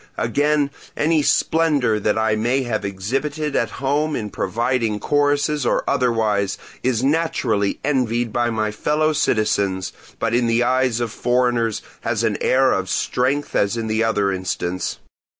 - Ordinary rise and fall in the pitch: Yes, average, 4.5 semitones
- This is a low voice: Yes, low, 120 Hz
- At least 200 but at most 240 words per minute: No, average, 150 wpm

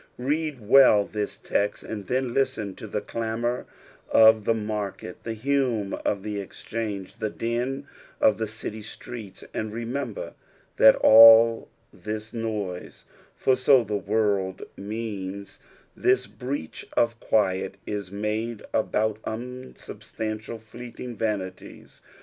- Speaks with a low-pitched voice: Yes, low, 110 Hz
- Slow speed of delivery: Yes, slow, 120 wpm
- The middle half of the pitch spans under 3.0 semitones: Yes, narrow, 2.4 semitones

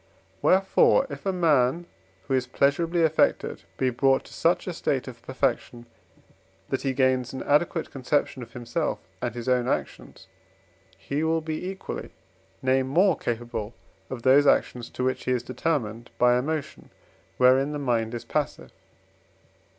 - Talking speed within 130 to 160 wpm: Yes, average, 150 wpm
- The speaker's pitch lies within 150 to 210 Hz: No, low, 130 Hz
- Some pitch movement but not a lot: Yes, average, 4.0 semitones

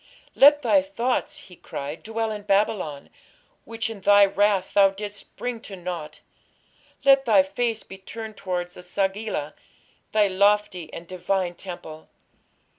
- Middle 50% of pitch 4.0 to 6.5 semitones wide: No, average, 3.4 semitones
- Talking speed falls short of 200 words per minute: Yes, average, 140 wpm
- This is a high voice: Yes, high, 200 Hz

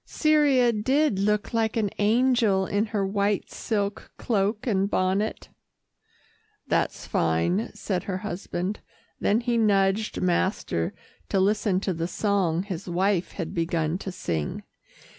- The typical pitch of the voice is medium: No, high, 200 Hz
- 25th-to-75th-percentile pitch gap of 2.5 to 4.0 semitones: Yes, average, 2.8 semitones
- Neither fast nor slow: No, slow, 130 wpm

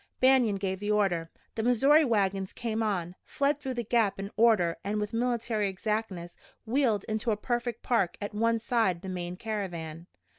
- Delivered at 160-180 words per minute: Yes, average, 175 wpm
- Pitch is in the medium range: No, high, 215 Hz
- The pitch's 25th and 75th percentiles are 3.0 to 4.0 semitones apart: Yes, average, 3.6 semitones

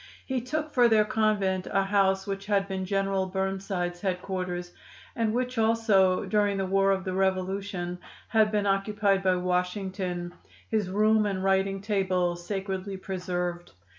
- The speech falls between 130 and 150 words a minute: Yes, average, 145 wpm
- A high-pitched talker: Yes, high, 195 Hz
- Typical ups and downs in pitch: No, narrow, 1.9 semitones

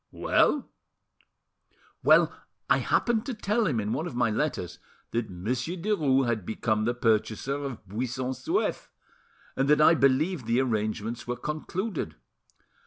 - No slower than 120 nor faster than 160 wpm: Yes, average, 140 wpm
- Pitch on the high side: No, low, 130 Hz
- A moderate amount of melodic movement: No, wide, 6.0 semitones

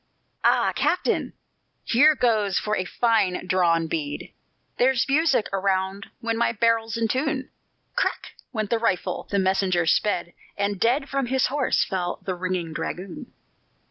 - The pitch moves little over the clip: No, average, 4.7 semitones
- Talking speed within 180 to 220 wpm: No, average, 140 wpm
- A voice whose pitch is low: No, high, 210 Hz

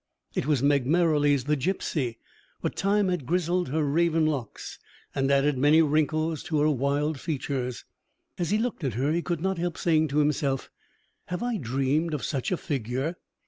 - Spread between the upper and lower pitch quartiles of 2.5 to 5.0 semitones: Yes, average, 3.6 semitones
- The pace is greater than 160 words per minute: Yes, average, 180 wpm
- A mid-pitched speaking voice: Yes, medium, 150 Hz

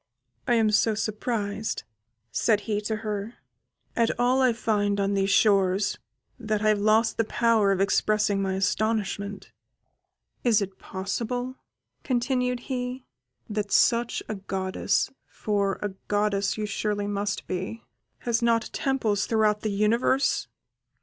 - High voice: Yes, high, 215 Hz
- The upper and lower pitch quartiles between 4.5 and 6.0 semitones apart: No, narrow, 2.4 semitones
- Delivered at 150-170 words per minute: No, slow, 135 wpm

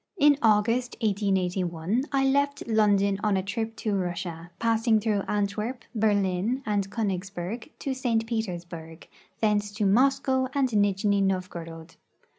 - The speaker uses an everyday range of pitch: Yes, average, 3.3 semitones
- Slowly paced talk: Yes, slow, 125 wpm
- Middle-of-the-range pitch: No, high, 210 Hz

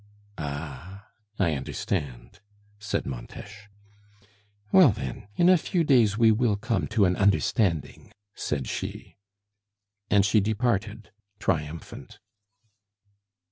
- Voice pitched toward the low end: Yes, low, 100 Hz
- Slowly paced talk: Yes, slow, 100 wpm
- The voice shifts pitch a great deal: Yes, wide, 6.1 semitones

